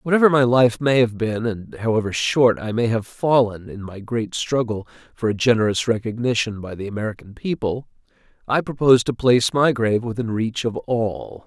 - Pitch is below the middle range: Yes, low, 115 Hz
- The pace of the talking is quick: No, average, 185 wpm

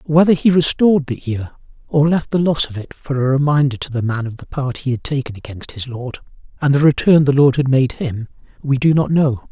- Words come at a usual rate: No, fast, 240 wpm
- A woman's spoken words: No, male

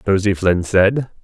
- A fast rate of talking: No, average, 145 wpm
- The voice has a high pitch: No, low, 100 Hz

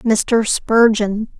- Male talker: No, female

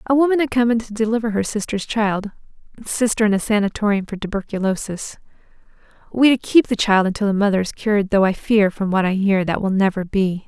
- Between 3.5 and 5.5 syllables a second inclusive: No, 5.9 syllables/s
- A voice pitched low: No, high, 210 Hz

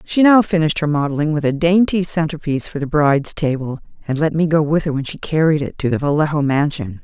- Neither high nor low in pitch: Yes, medium, 150 Hz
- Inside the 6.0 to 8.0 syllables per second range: Yes, 6.2 syllables/s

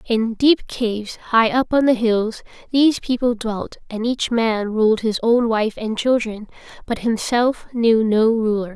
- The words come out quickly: No, average, 170 wpm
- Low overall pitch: No, high, 230 Hz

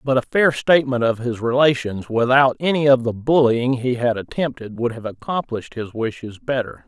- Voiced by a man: Yes, male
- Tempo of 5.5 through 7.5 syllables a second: No, 5.2 syllables/s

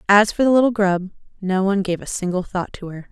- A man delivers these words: No, female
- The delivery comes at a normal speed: No, fast, 250 wpm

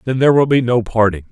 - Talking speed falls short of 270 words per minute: No, fast, 275 wpm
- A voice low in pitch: Yes, low, 120 Hz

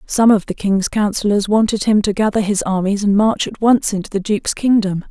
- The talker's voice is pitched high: Yes, high, 205 Hz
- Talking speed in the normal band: No, fast, 225 wpm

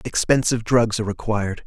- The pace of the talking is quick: No, average, 145 wpm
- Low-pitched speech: Yes, low, 110 Hz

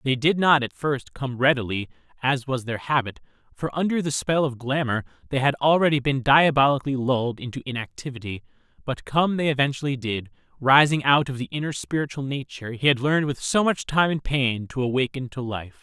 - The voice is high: No, low, 135 Hz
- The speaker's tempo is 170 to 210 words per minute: Yes, average, 190 wpm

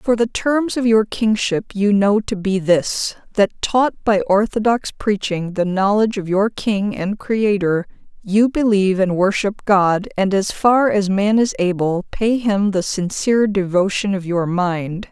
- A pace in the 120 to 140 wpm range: No, average, 170 wpm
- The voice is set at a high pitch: Yes, high, 200 Hz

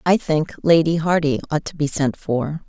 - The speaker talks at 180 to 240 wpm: Yes, average, 200 wpm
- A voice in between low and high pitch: Yes, medium, 155 Hz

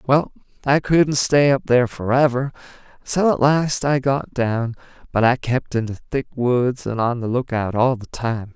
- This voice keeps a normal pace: Yes, average, 190 wpm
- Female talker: No, male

